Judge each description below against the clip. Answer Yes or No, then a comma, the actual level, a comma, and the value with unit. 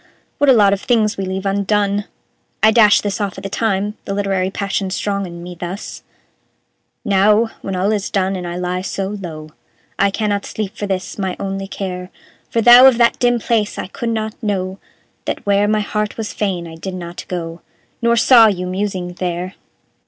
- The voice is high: Yes, high, 200 Hz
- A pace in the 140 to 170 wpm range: No, average, 195 wpm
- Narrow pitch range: Yes, narrow, 2.3 semitones